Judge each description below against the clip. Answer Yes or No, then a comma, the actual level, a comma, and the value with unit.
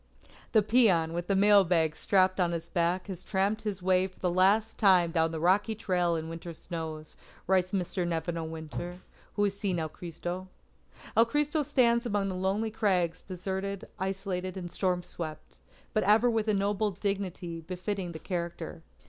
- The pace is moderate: Yes, average, 180 wpm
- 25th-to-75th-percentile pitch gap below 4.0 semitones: Yes, average, 2.9 semitones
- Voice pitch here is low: No, medium, 185 Hz